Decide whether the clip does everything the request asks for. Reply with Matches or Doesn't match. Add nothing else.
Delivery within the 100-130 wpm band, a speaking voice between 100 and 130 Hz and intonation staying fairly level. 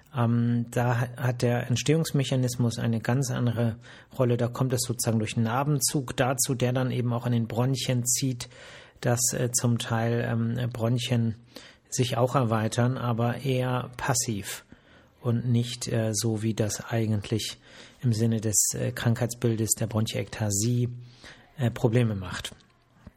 Matches